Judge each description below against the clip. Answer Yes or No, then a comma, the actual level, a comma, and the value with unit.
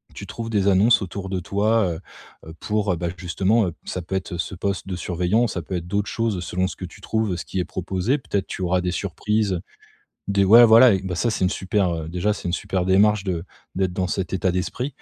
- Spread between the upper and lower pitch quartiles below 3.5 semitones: Yes, average, 2.8 semitones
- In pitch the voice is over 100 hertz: No, very low, 95 Hz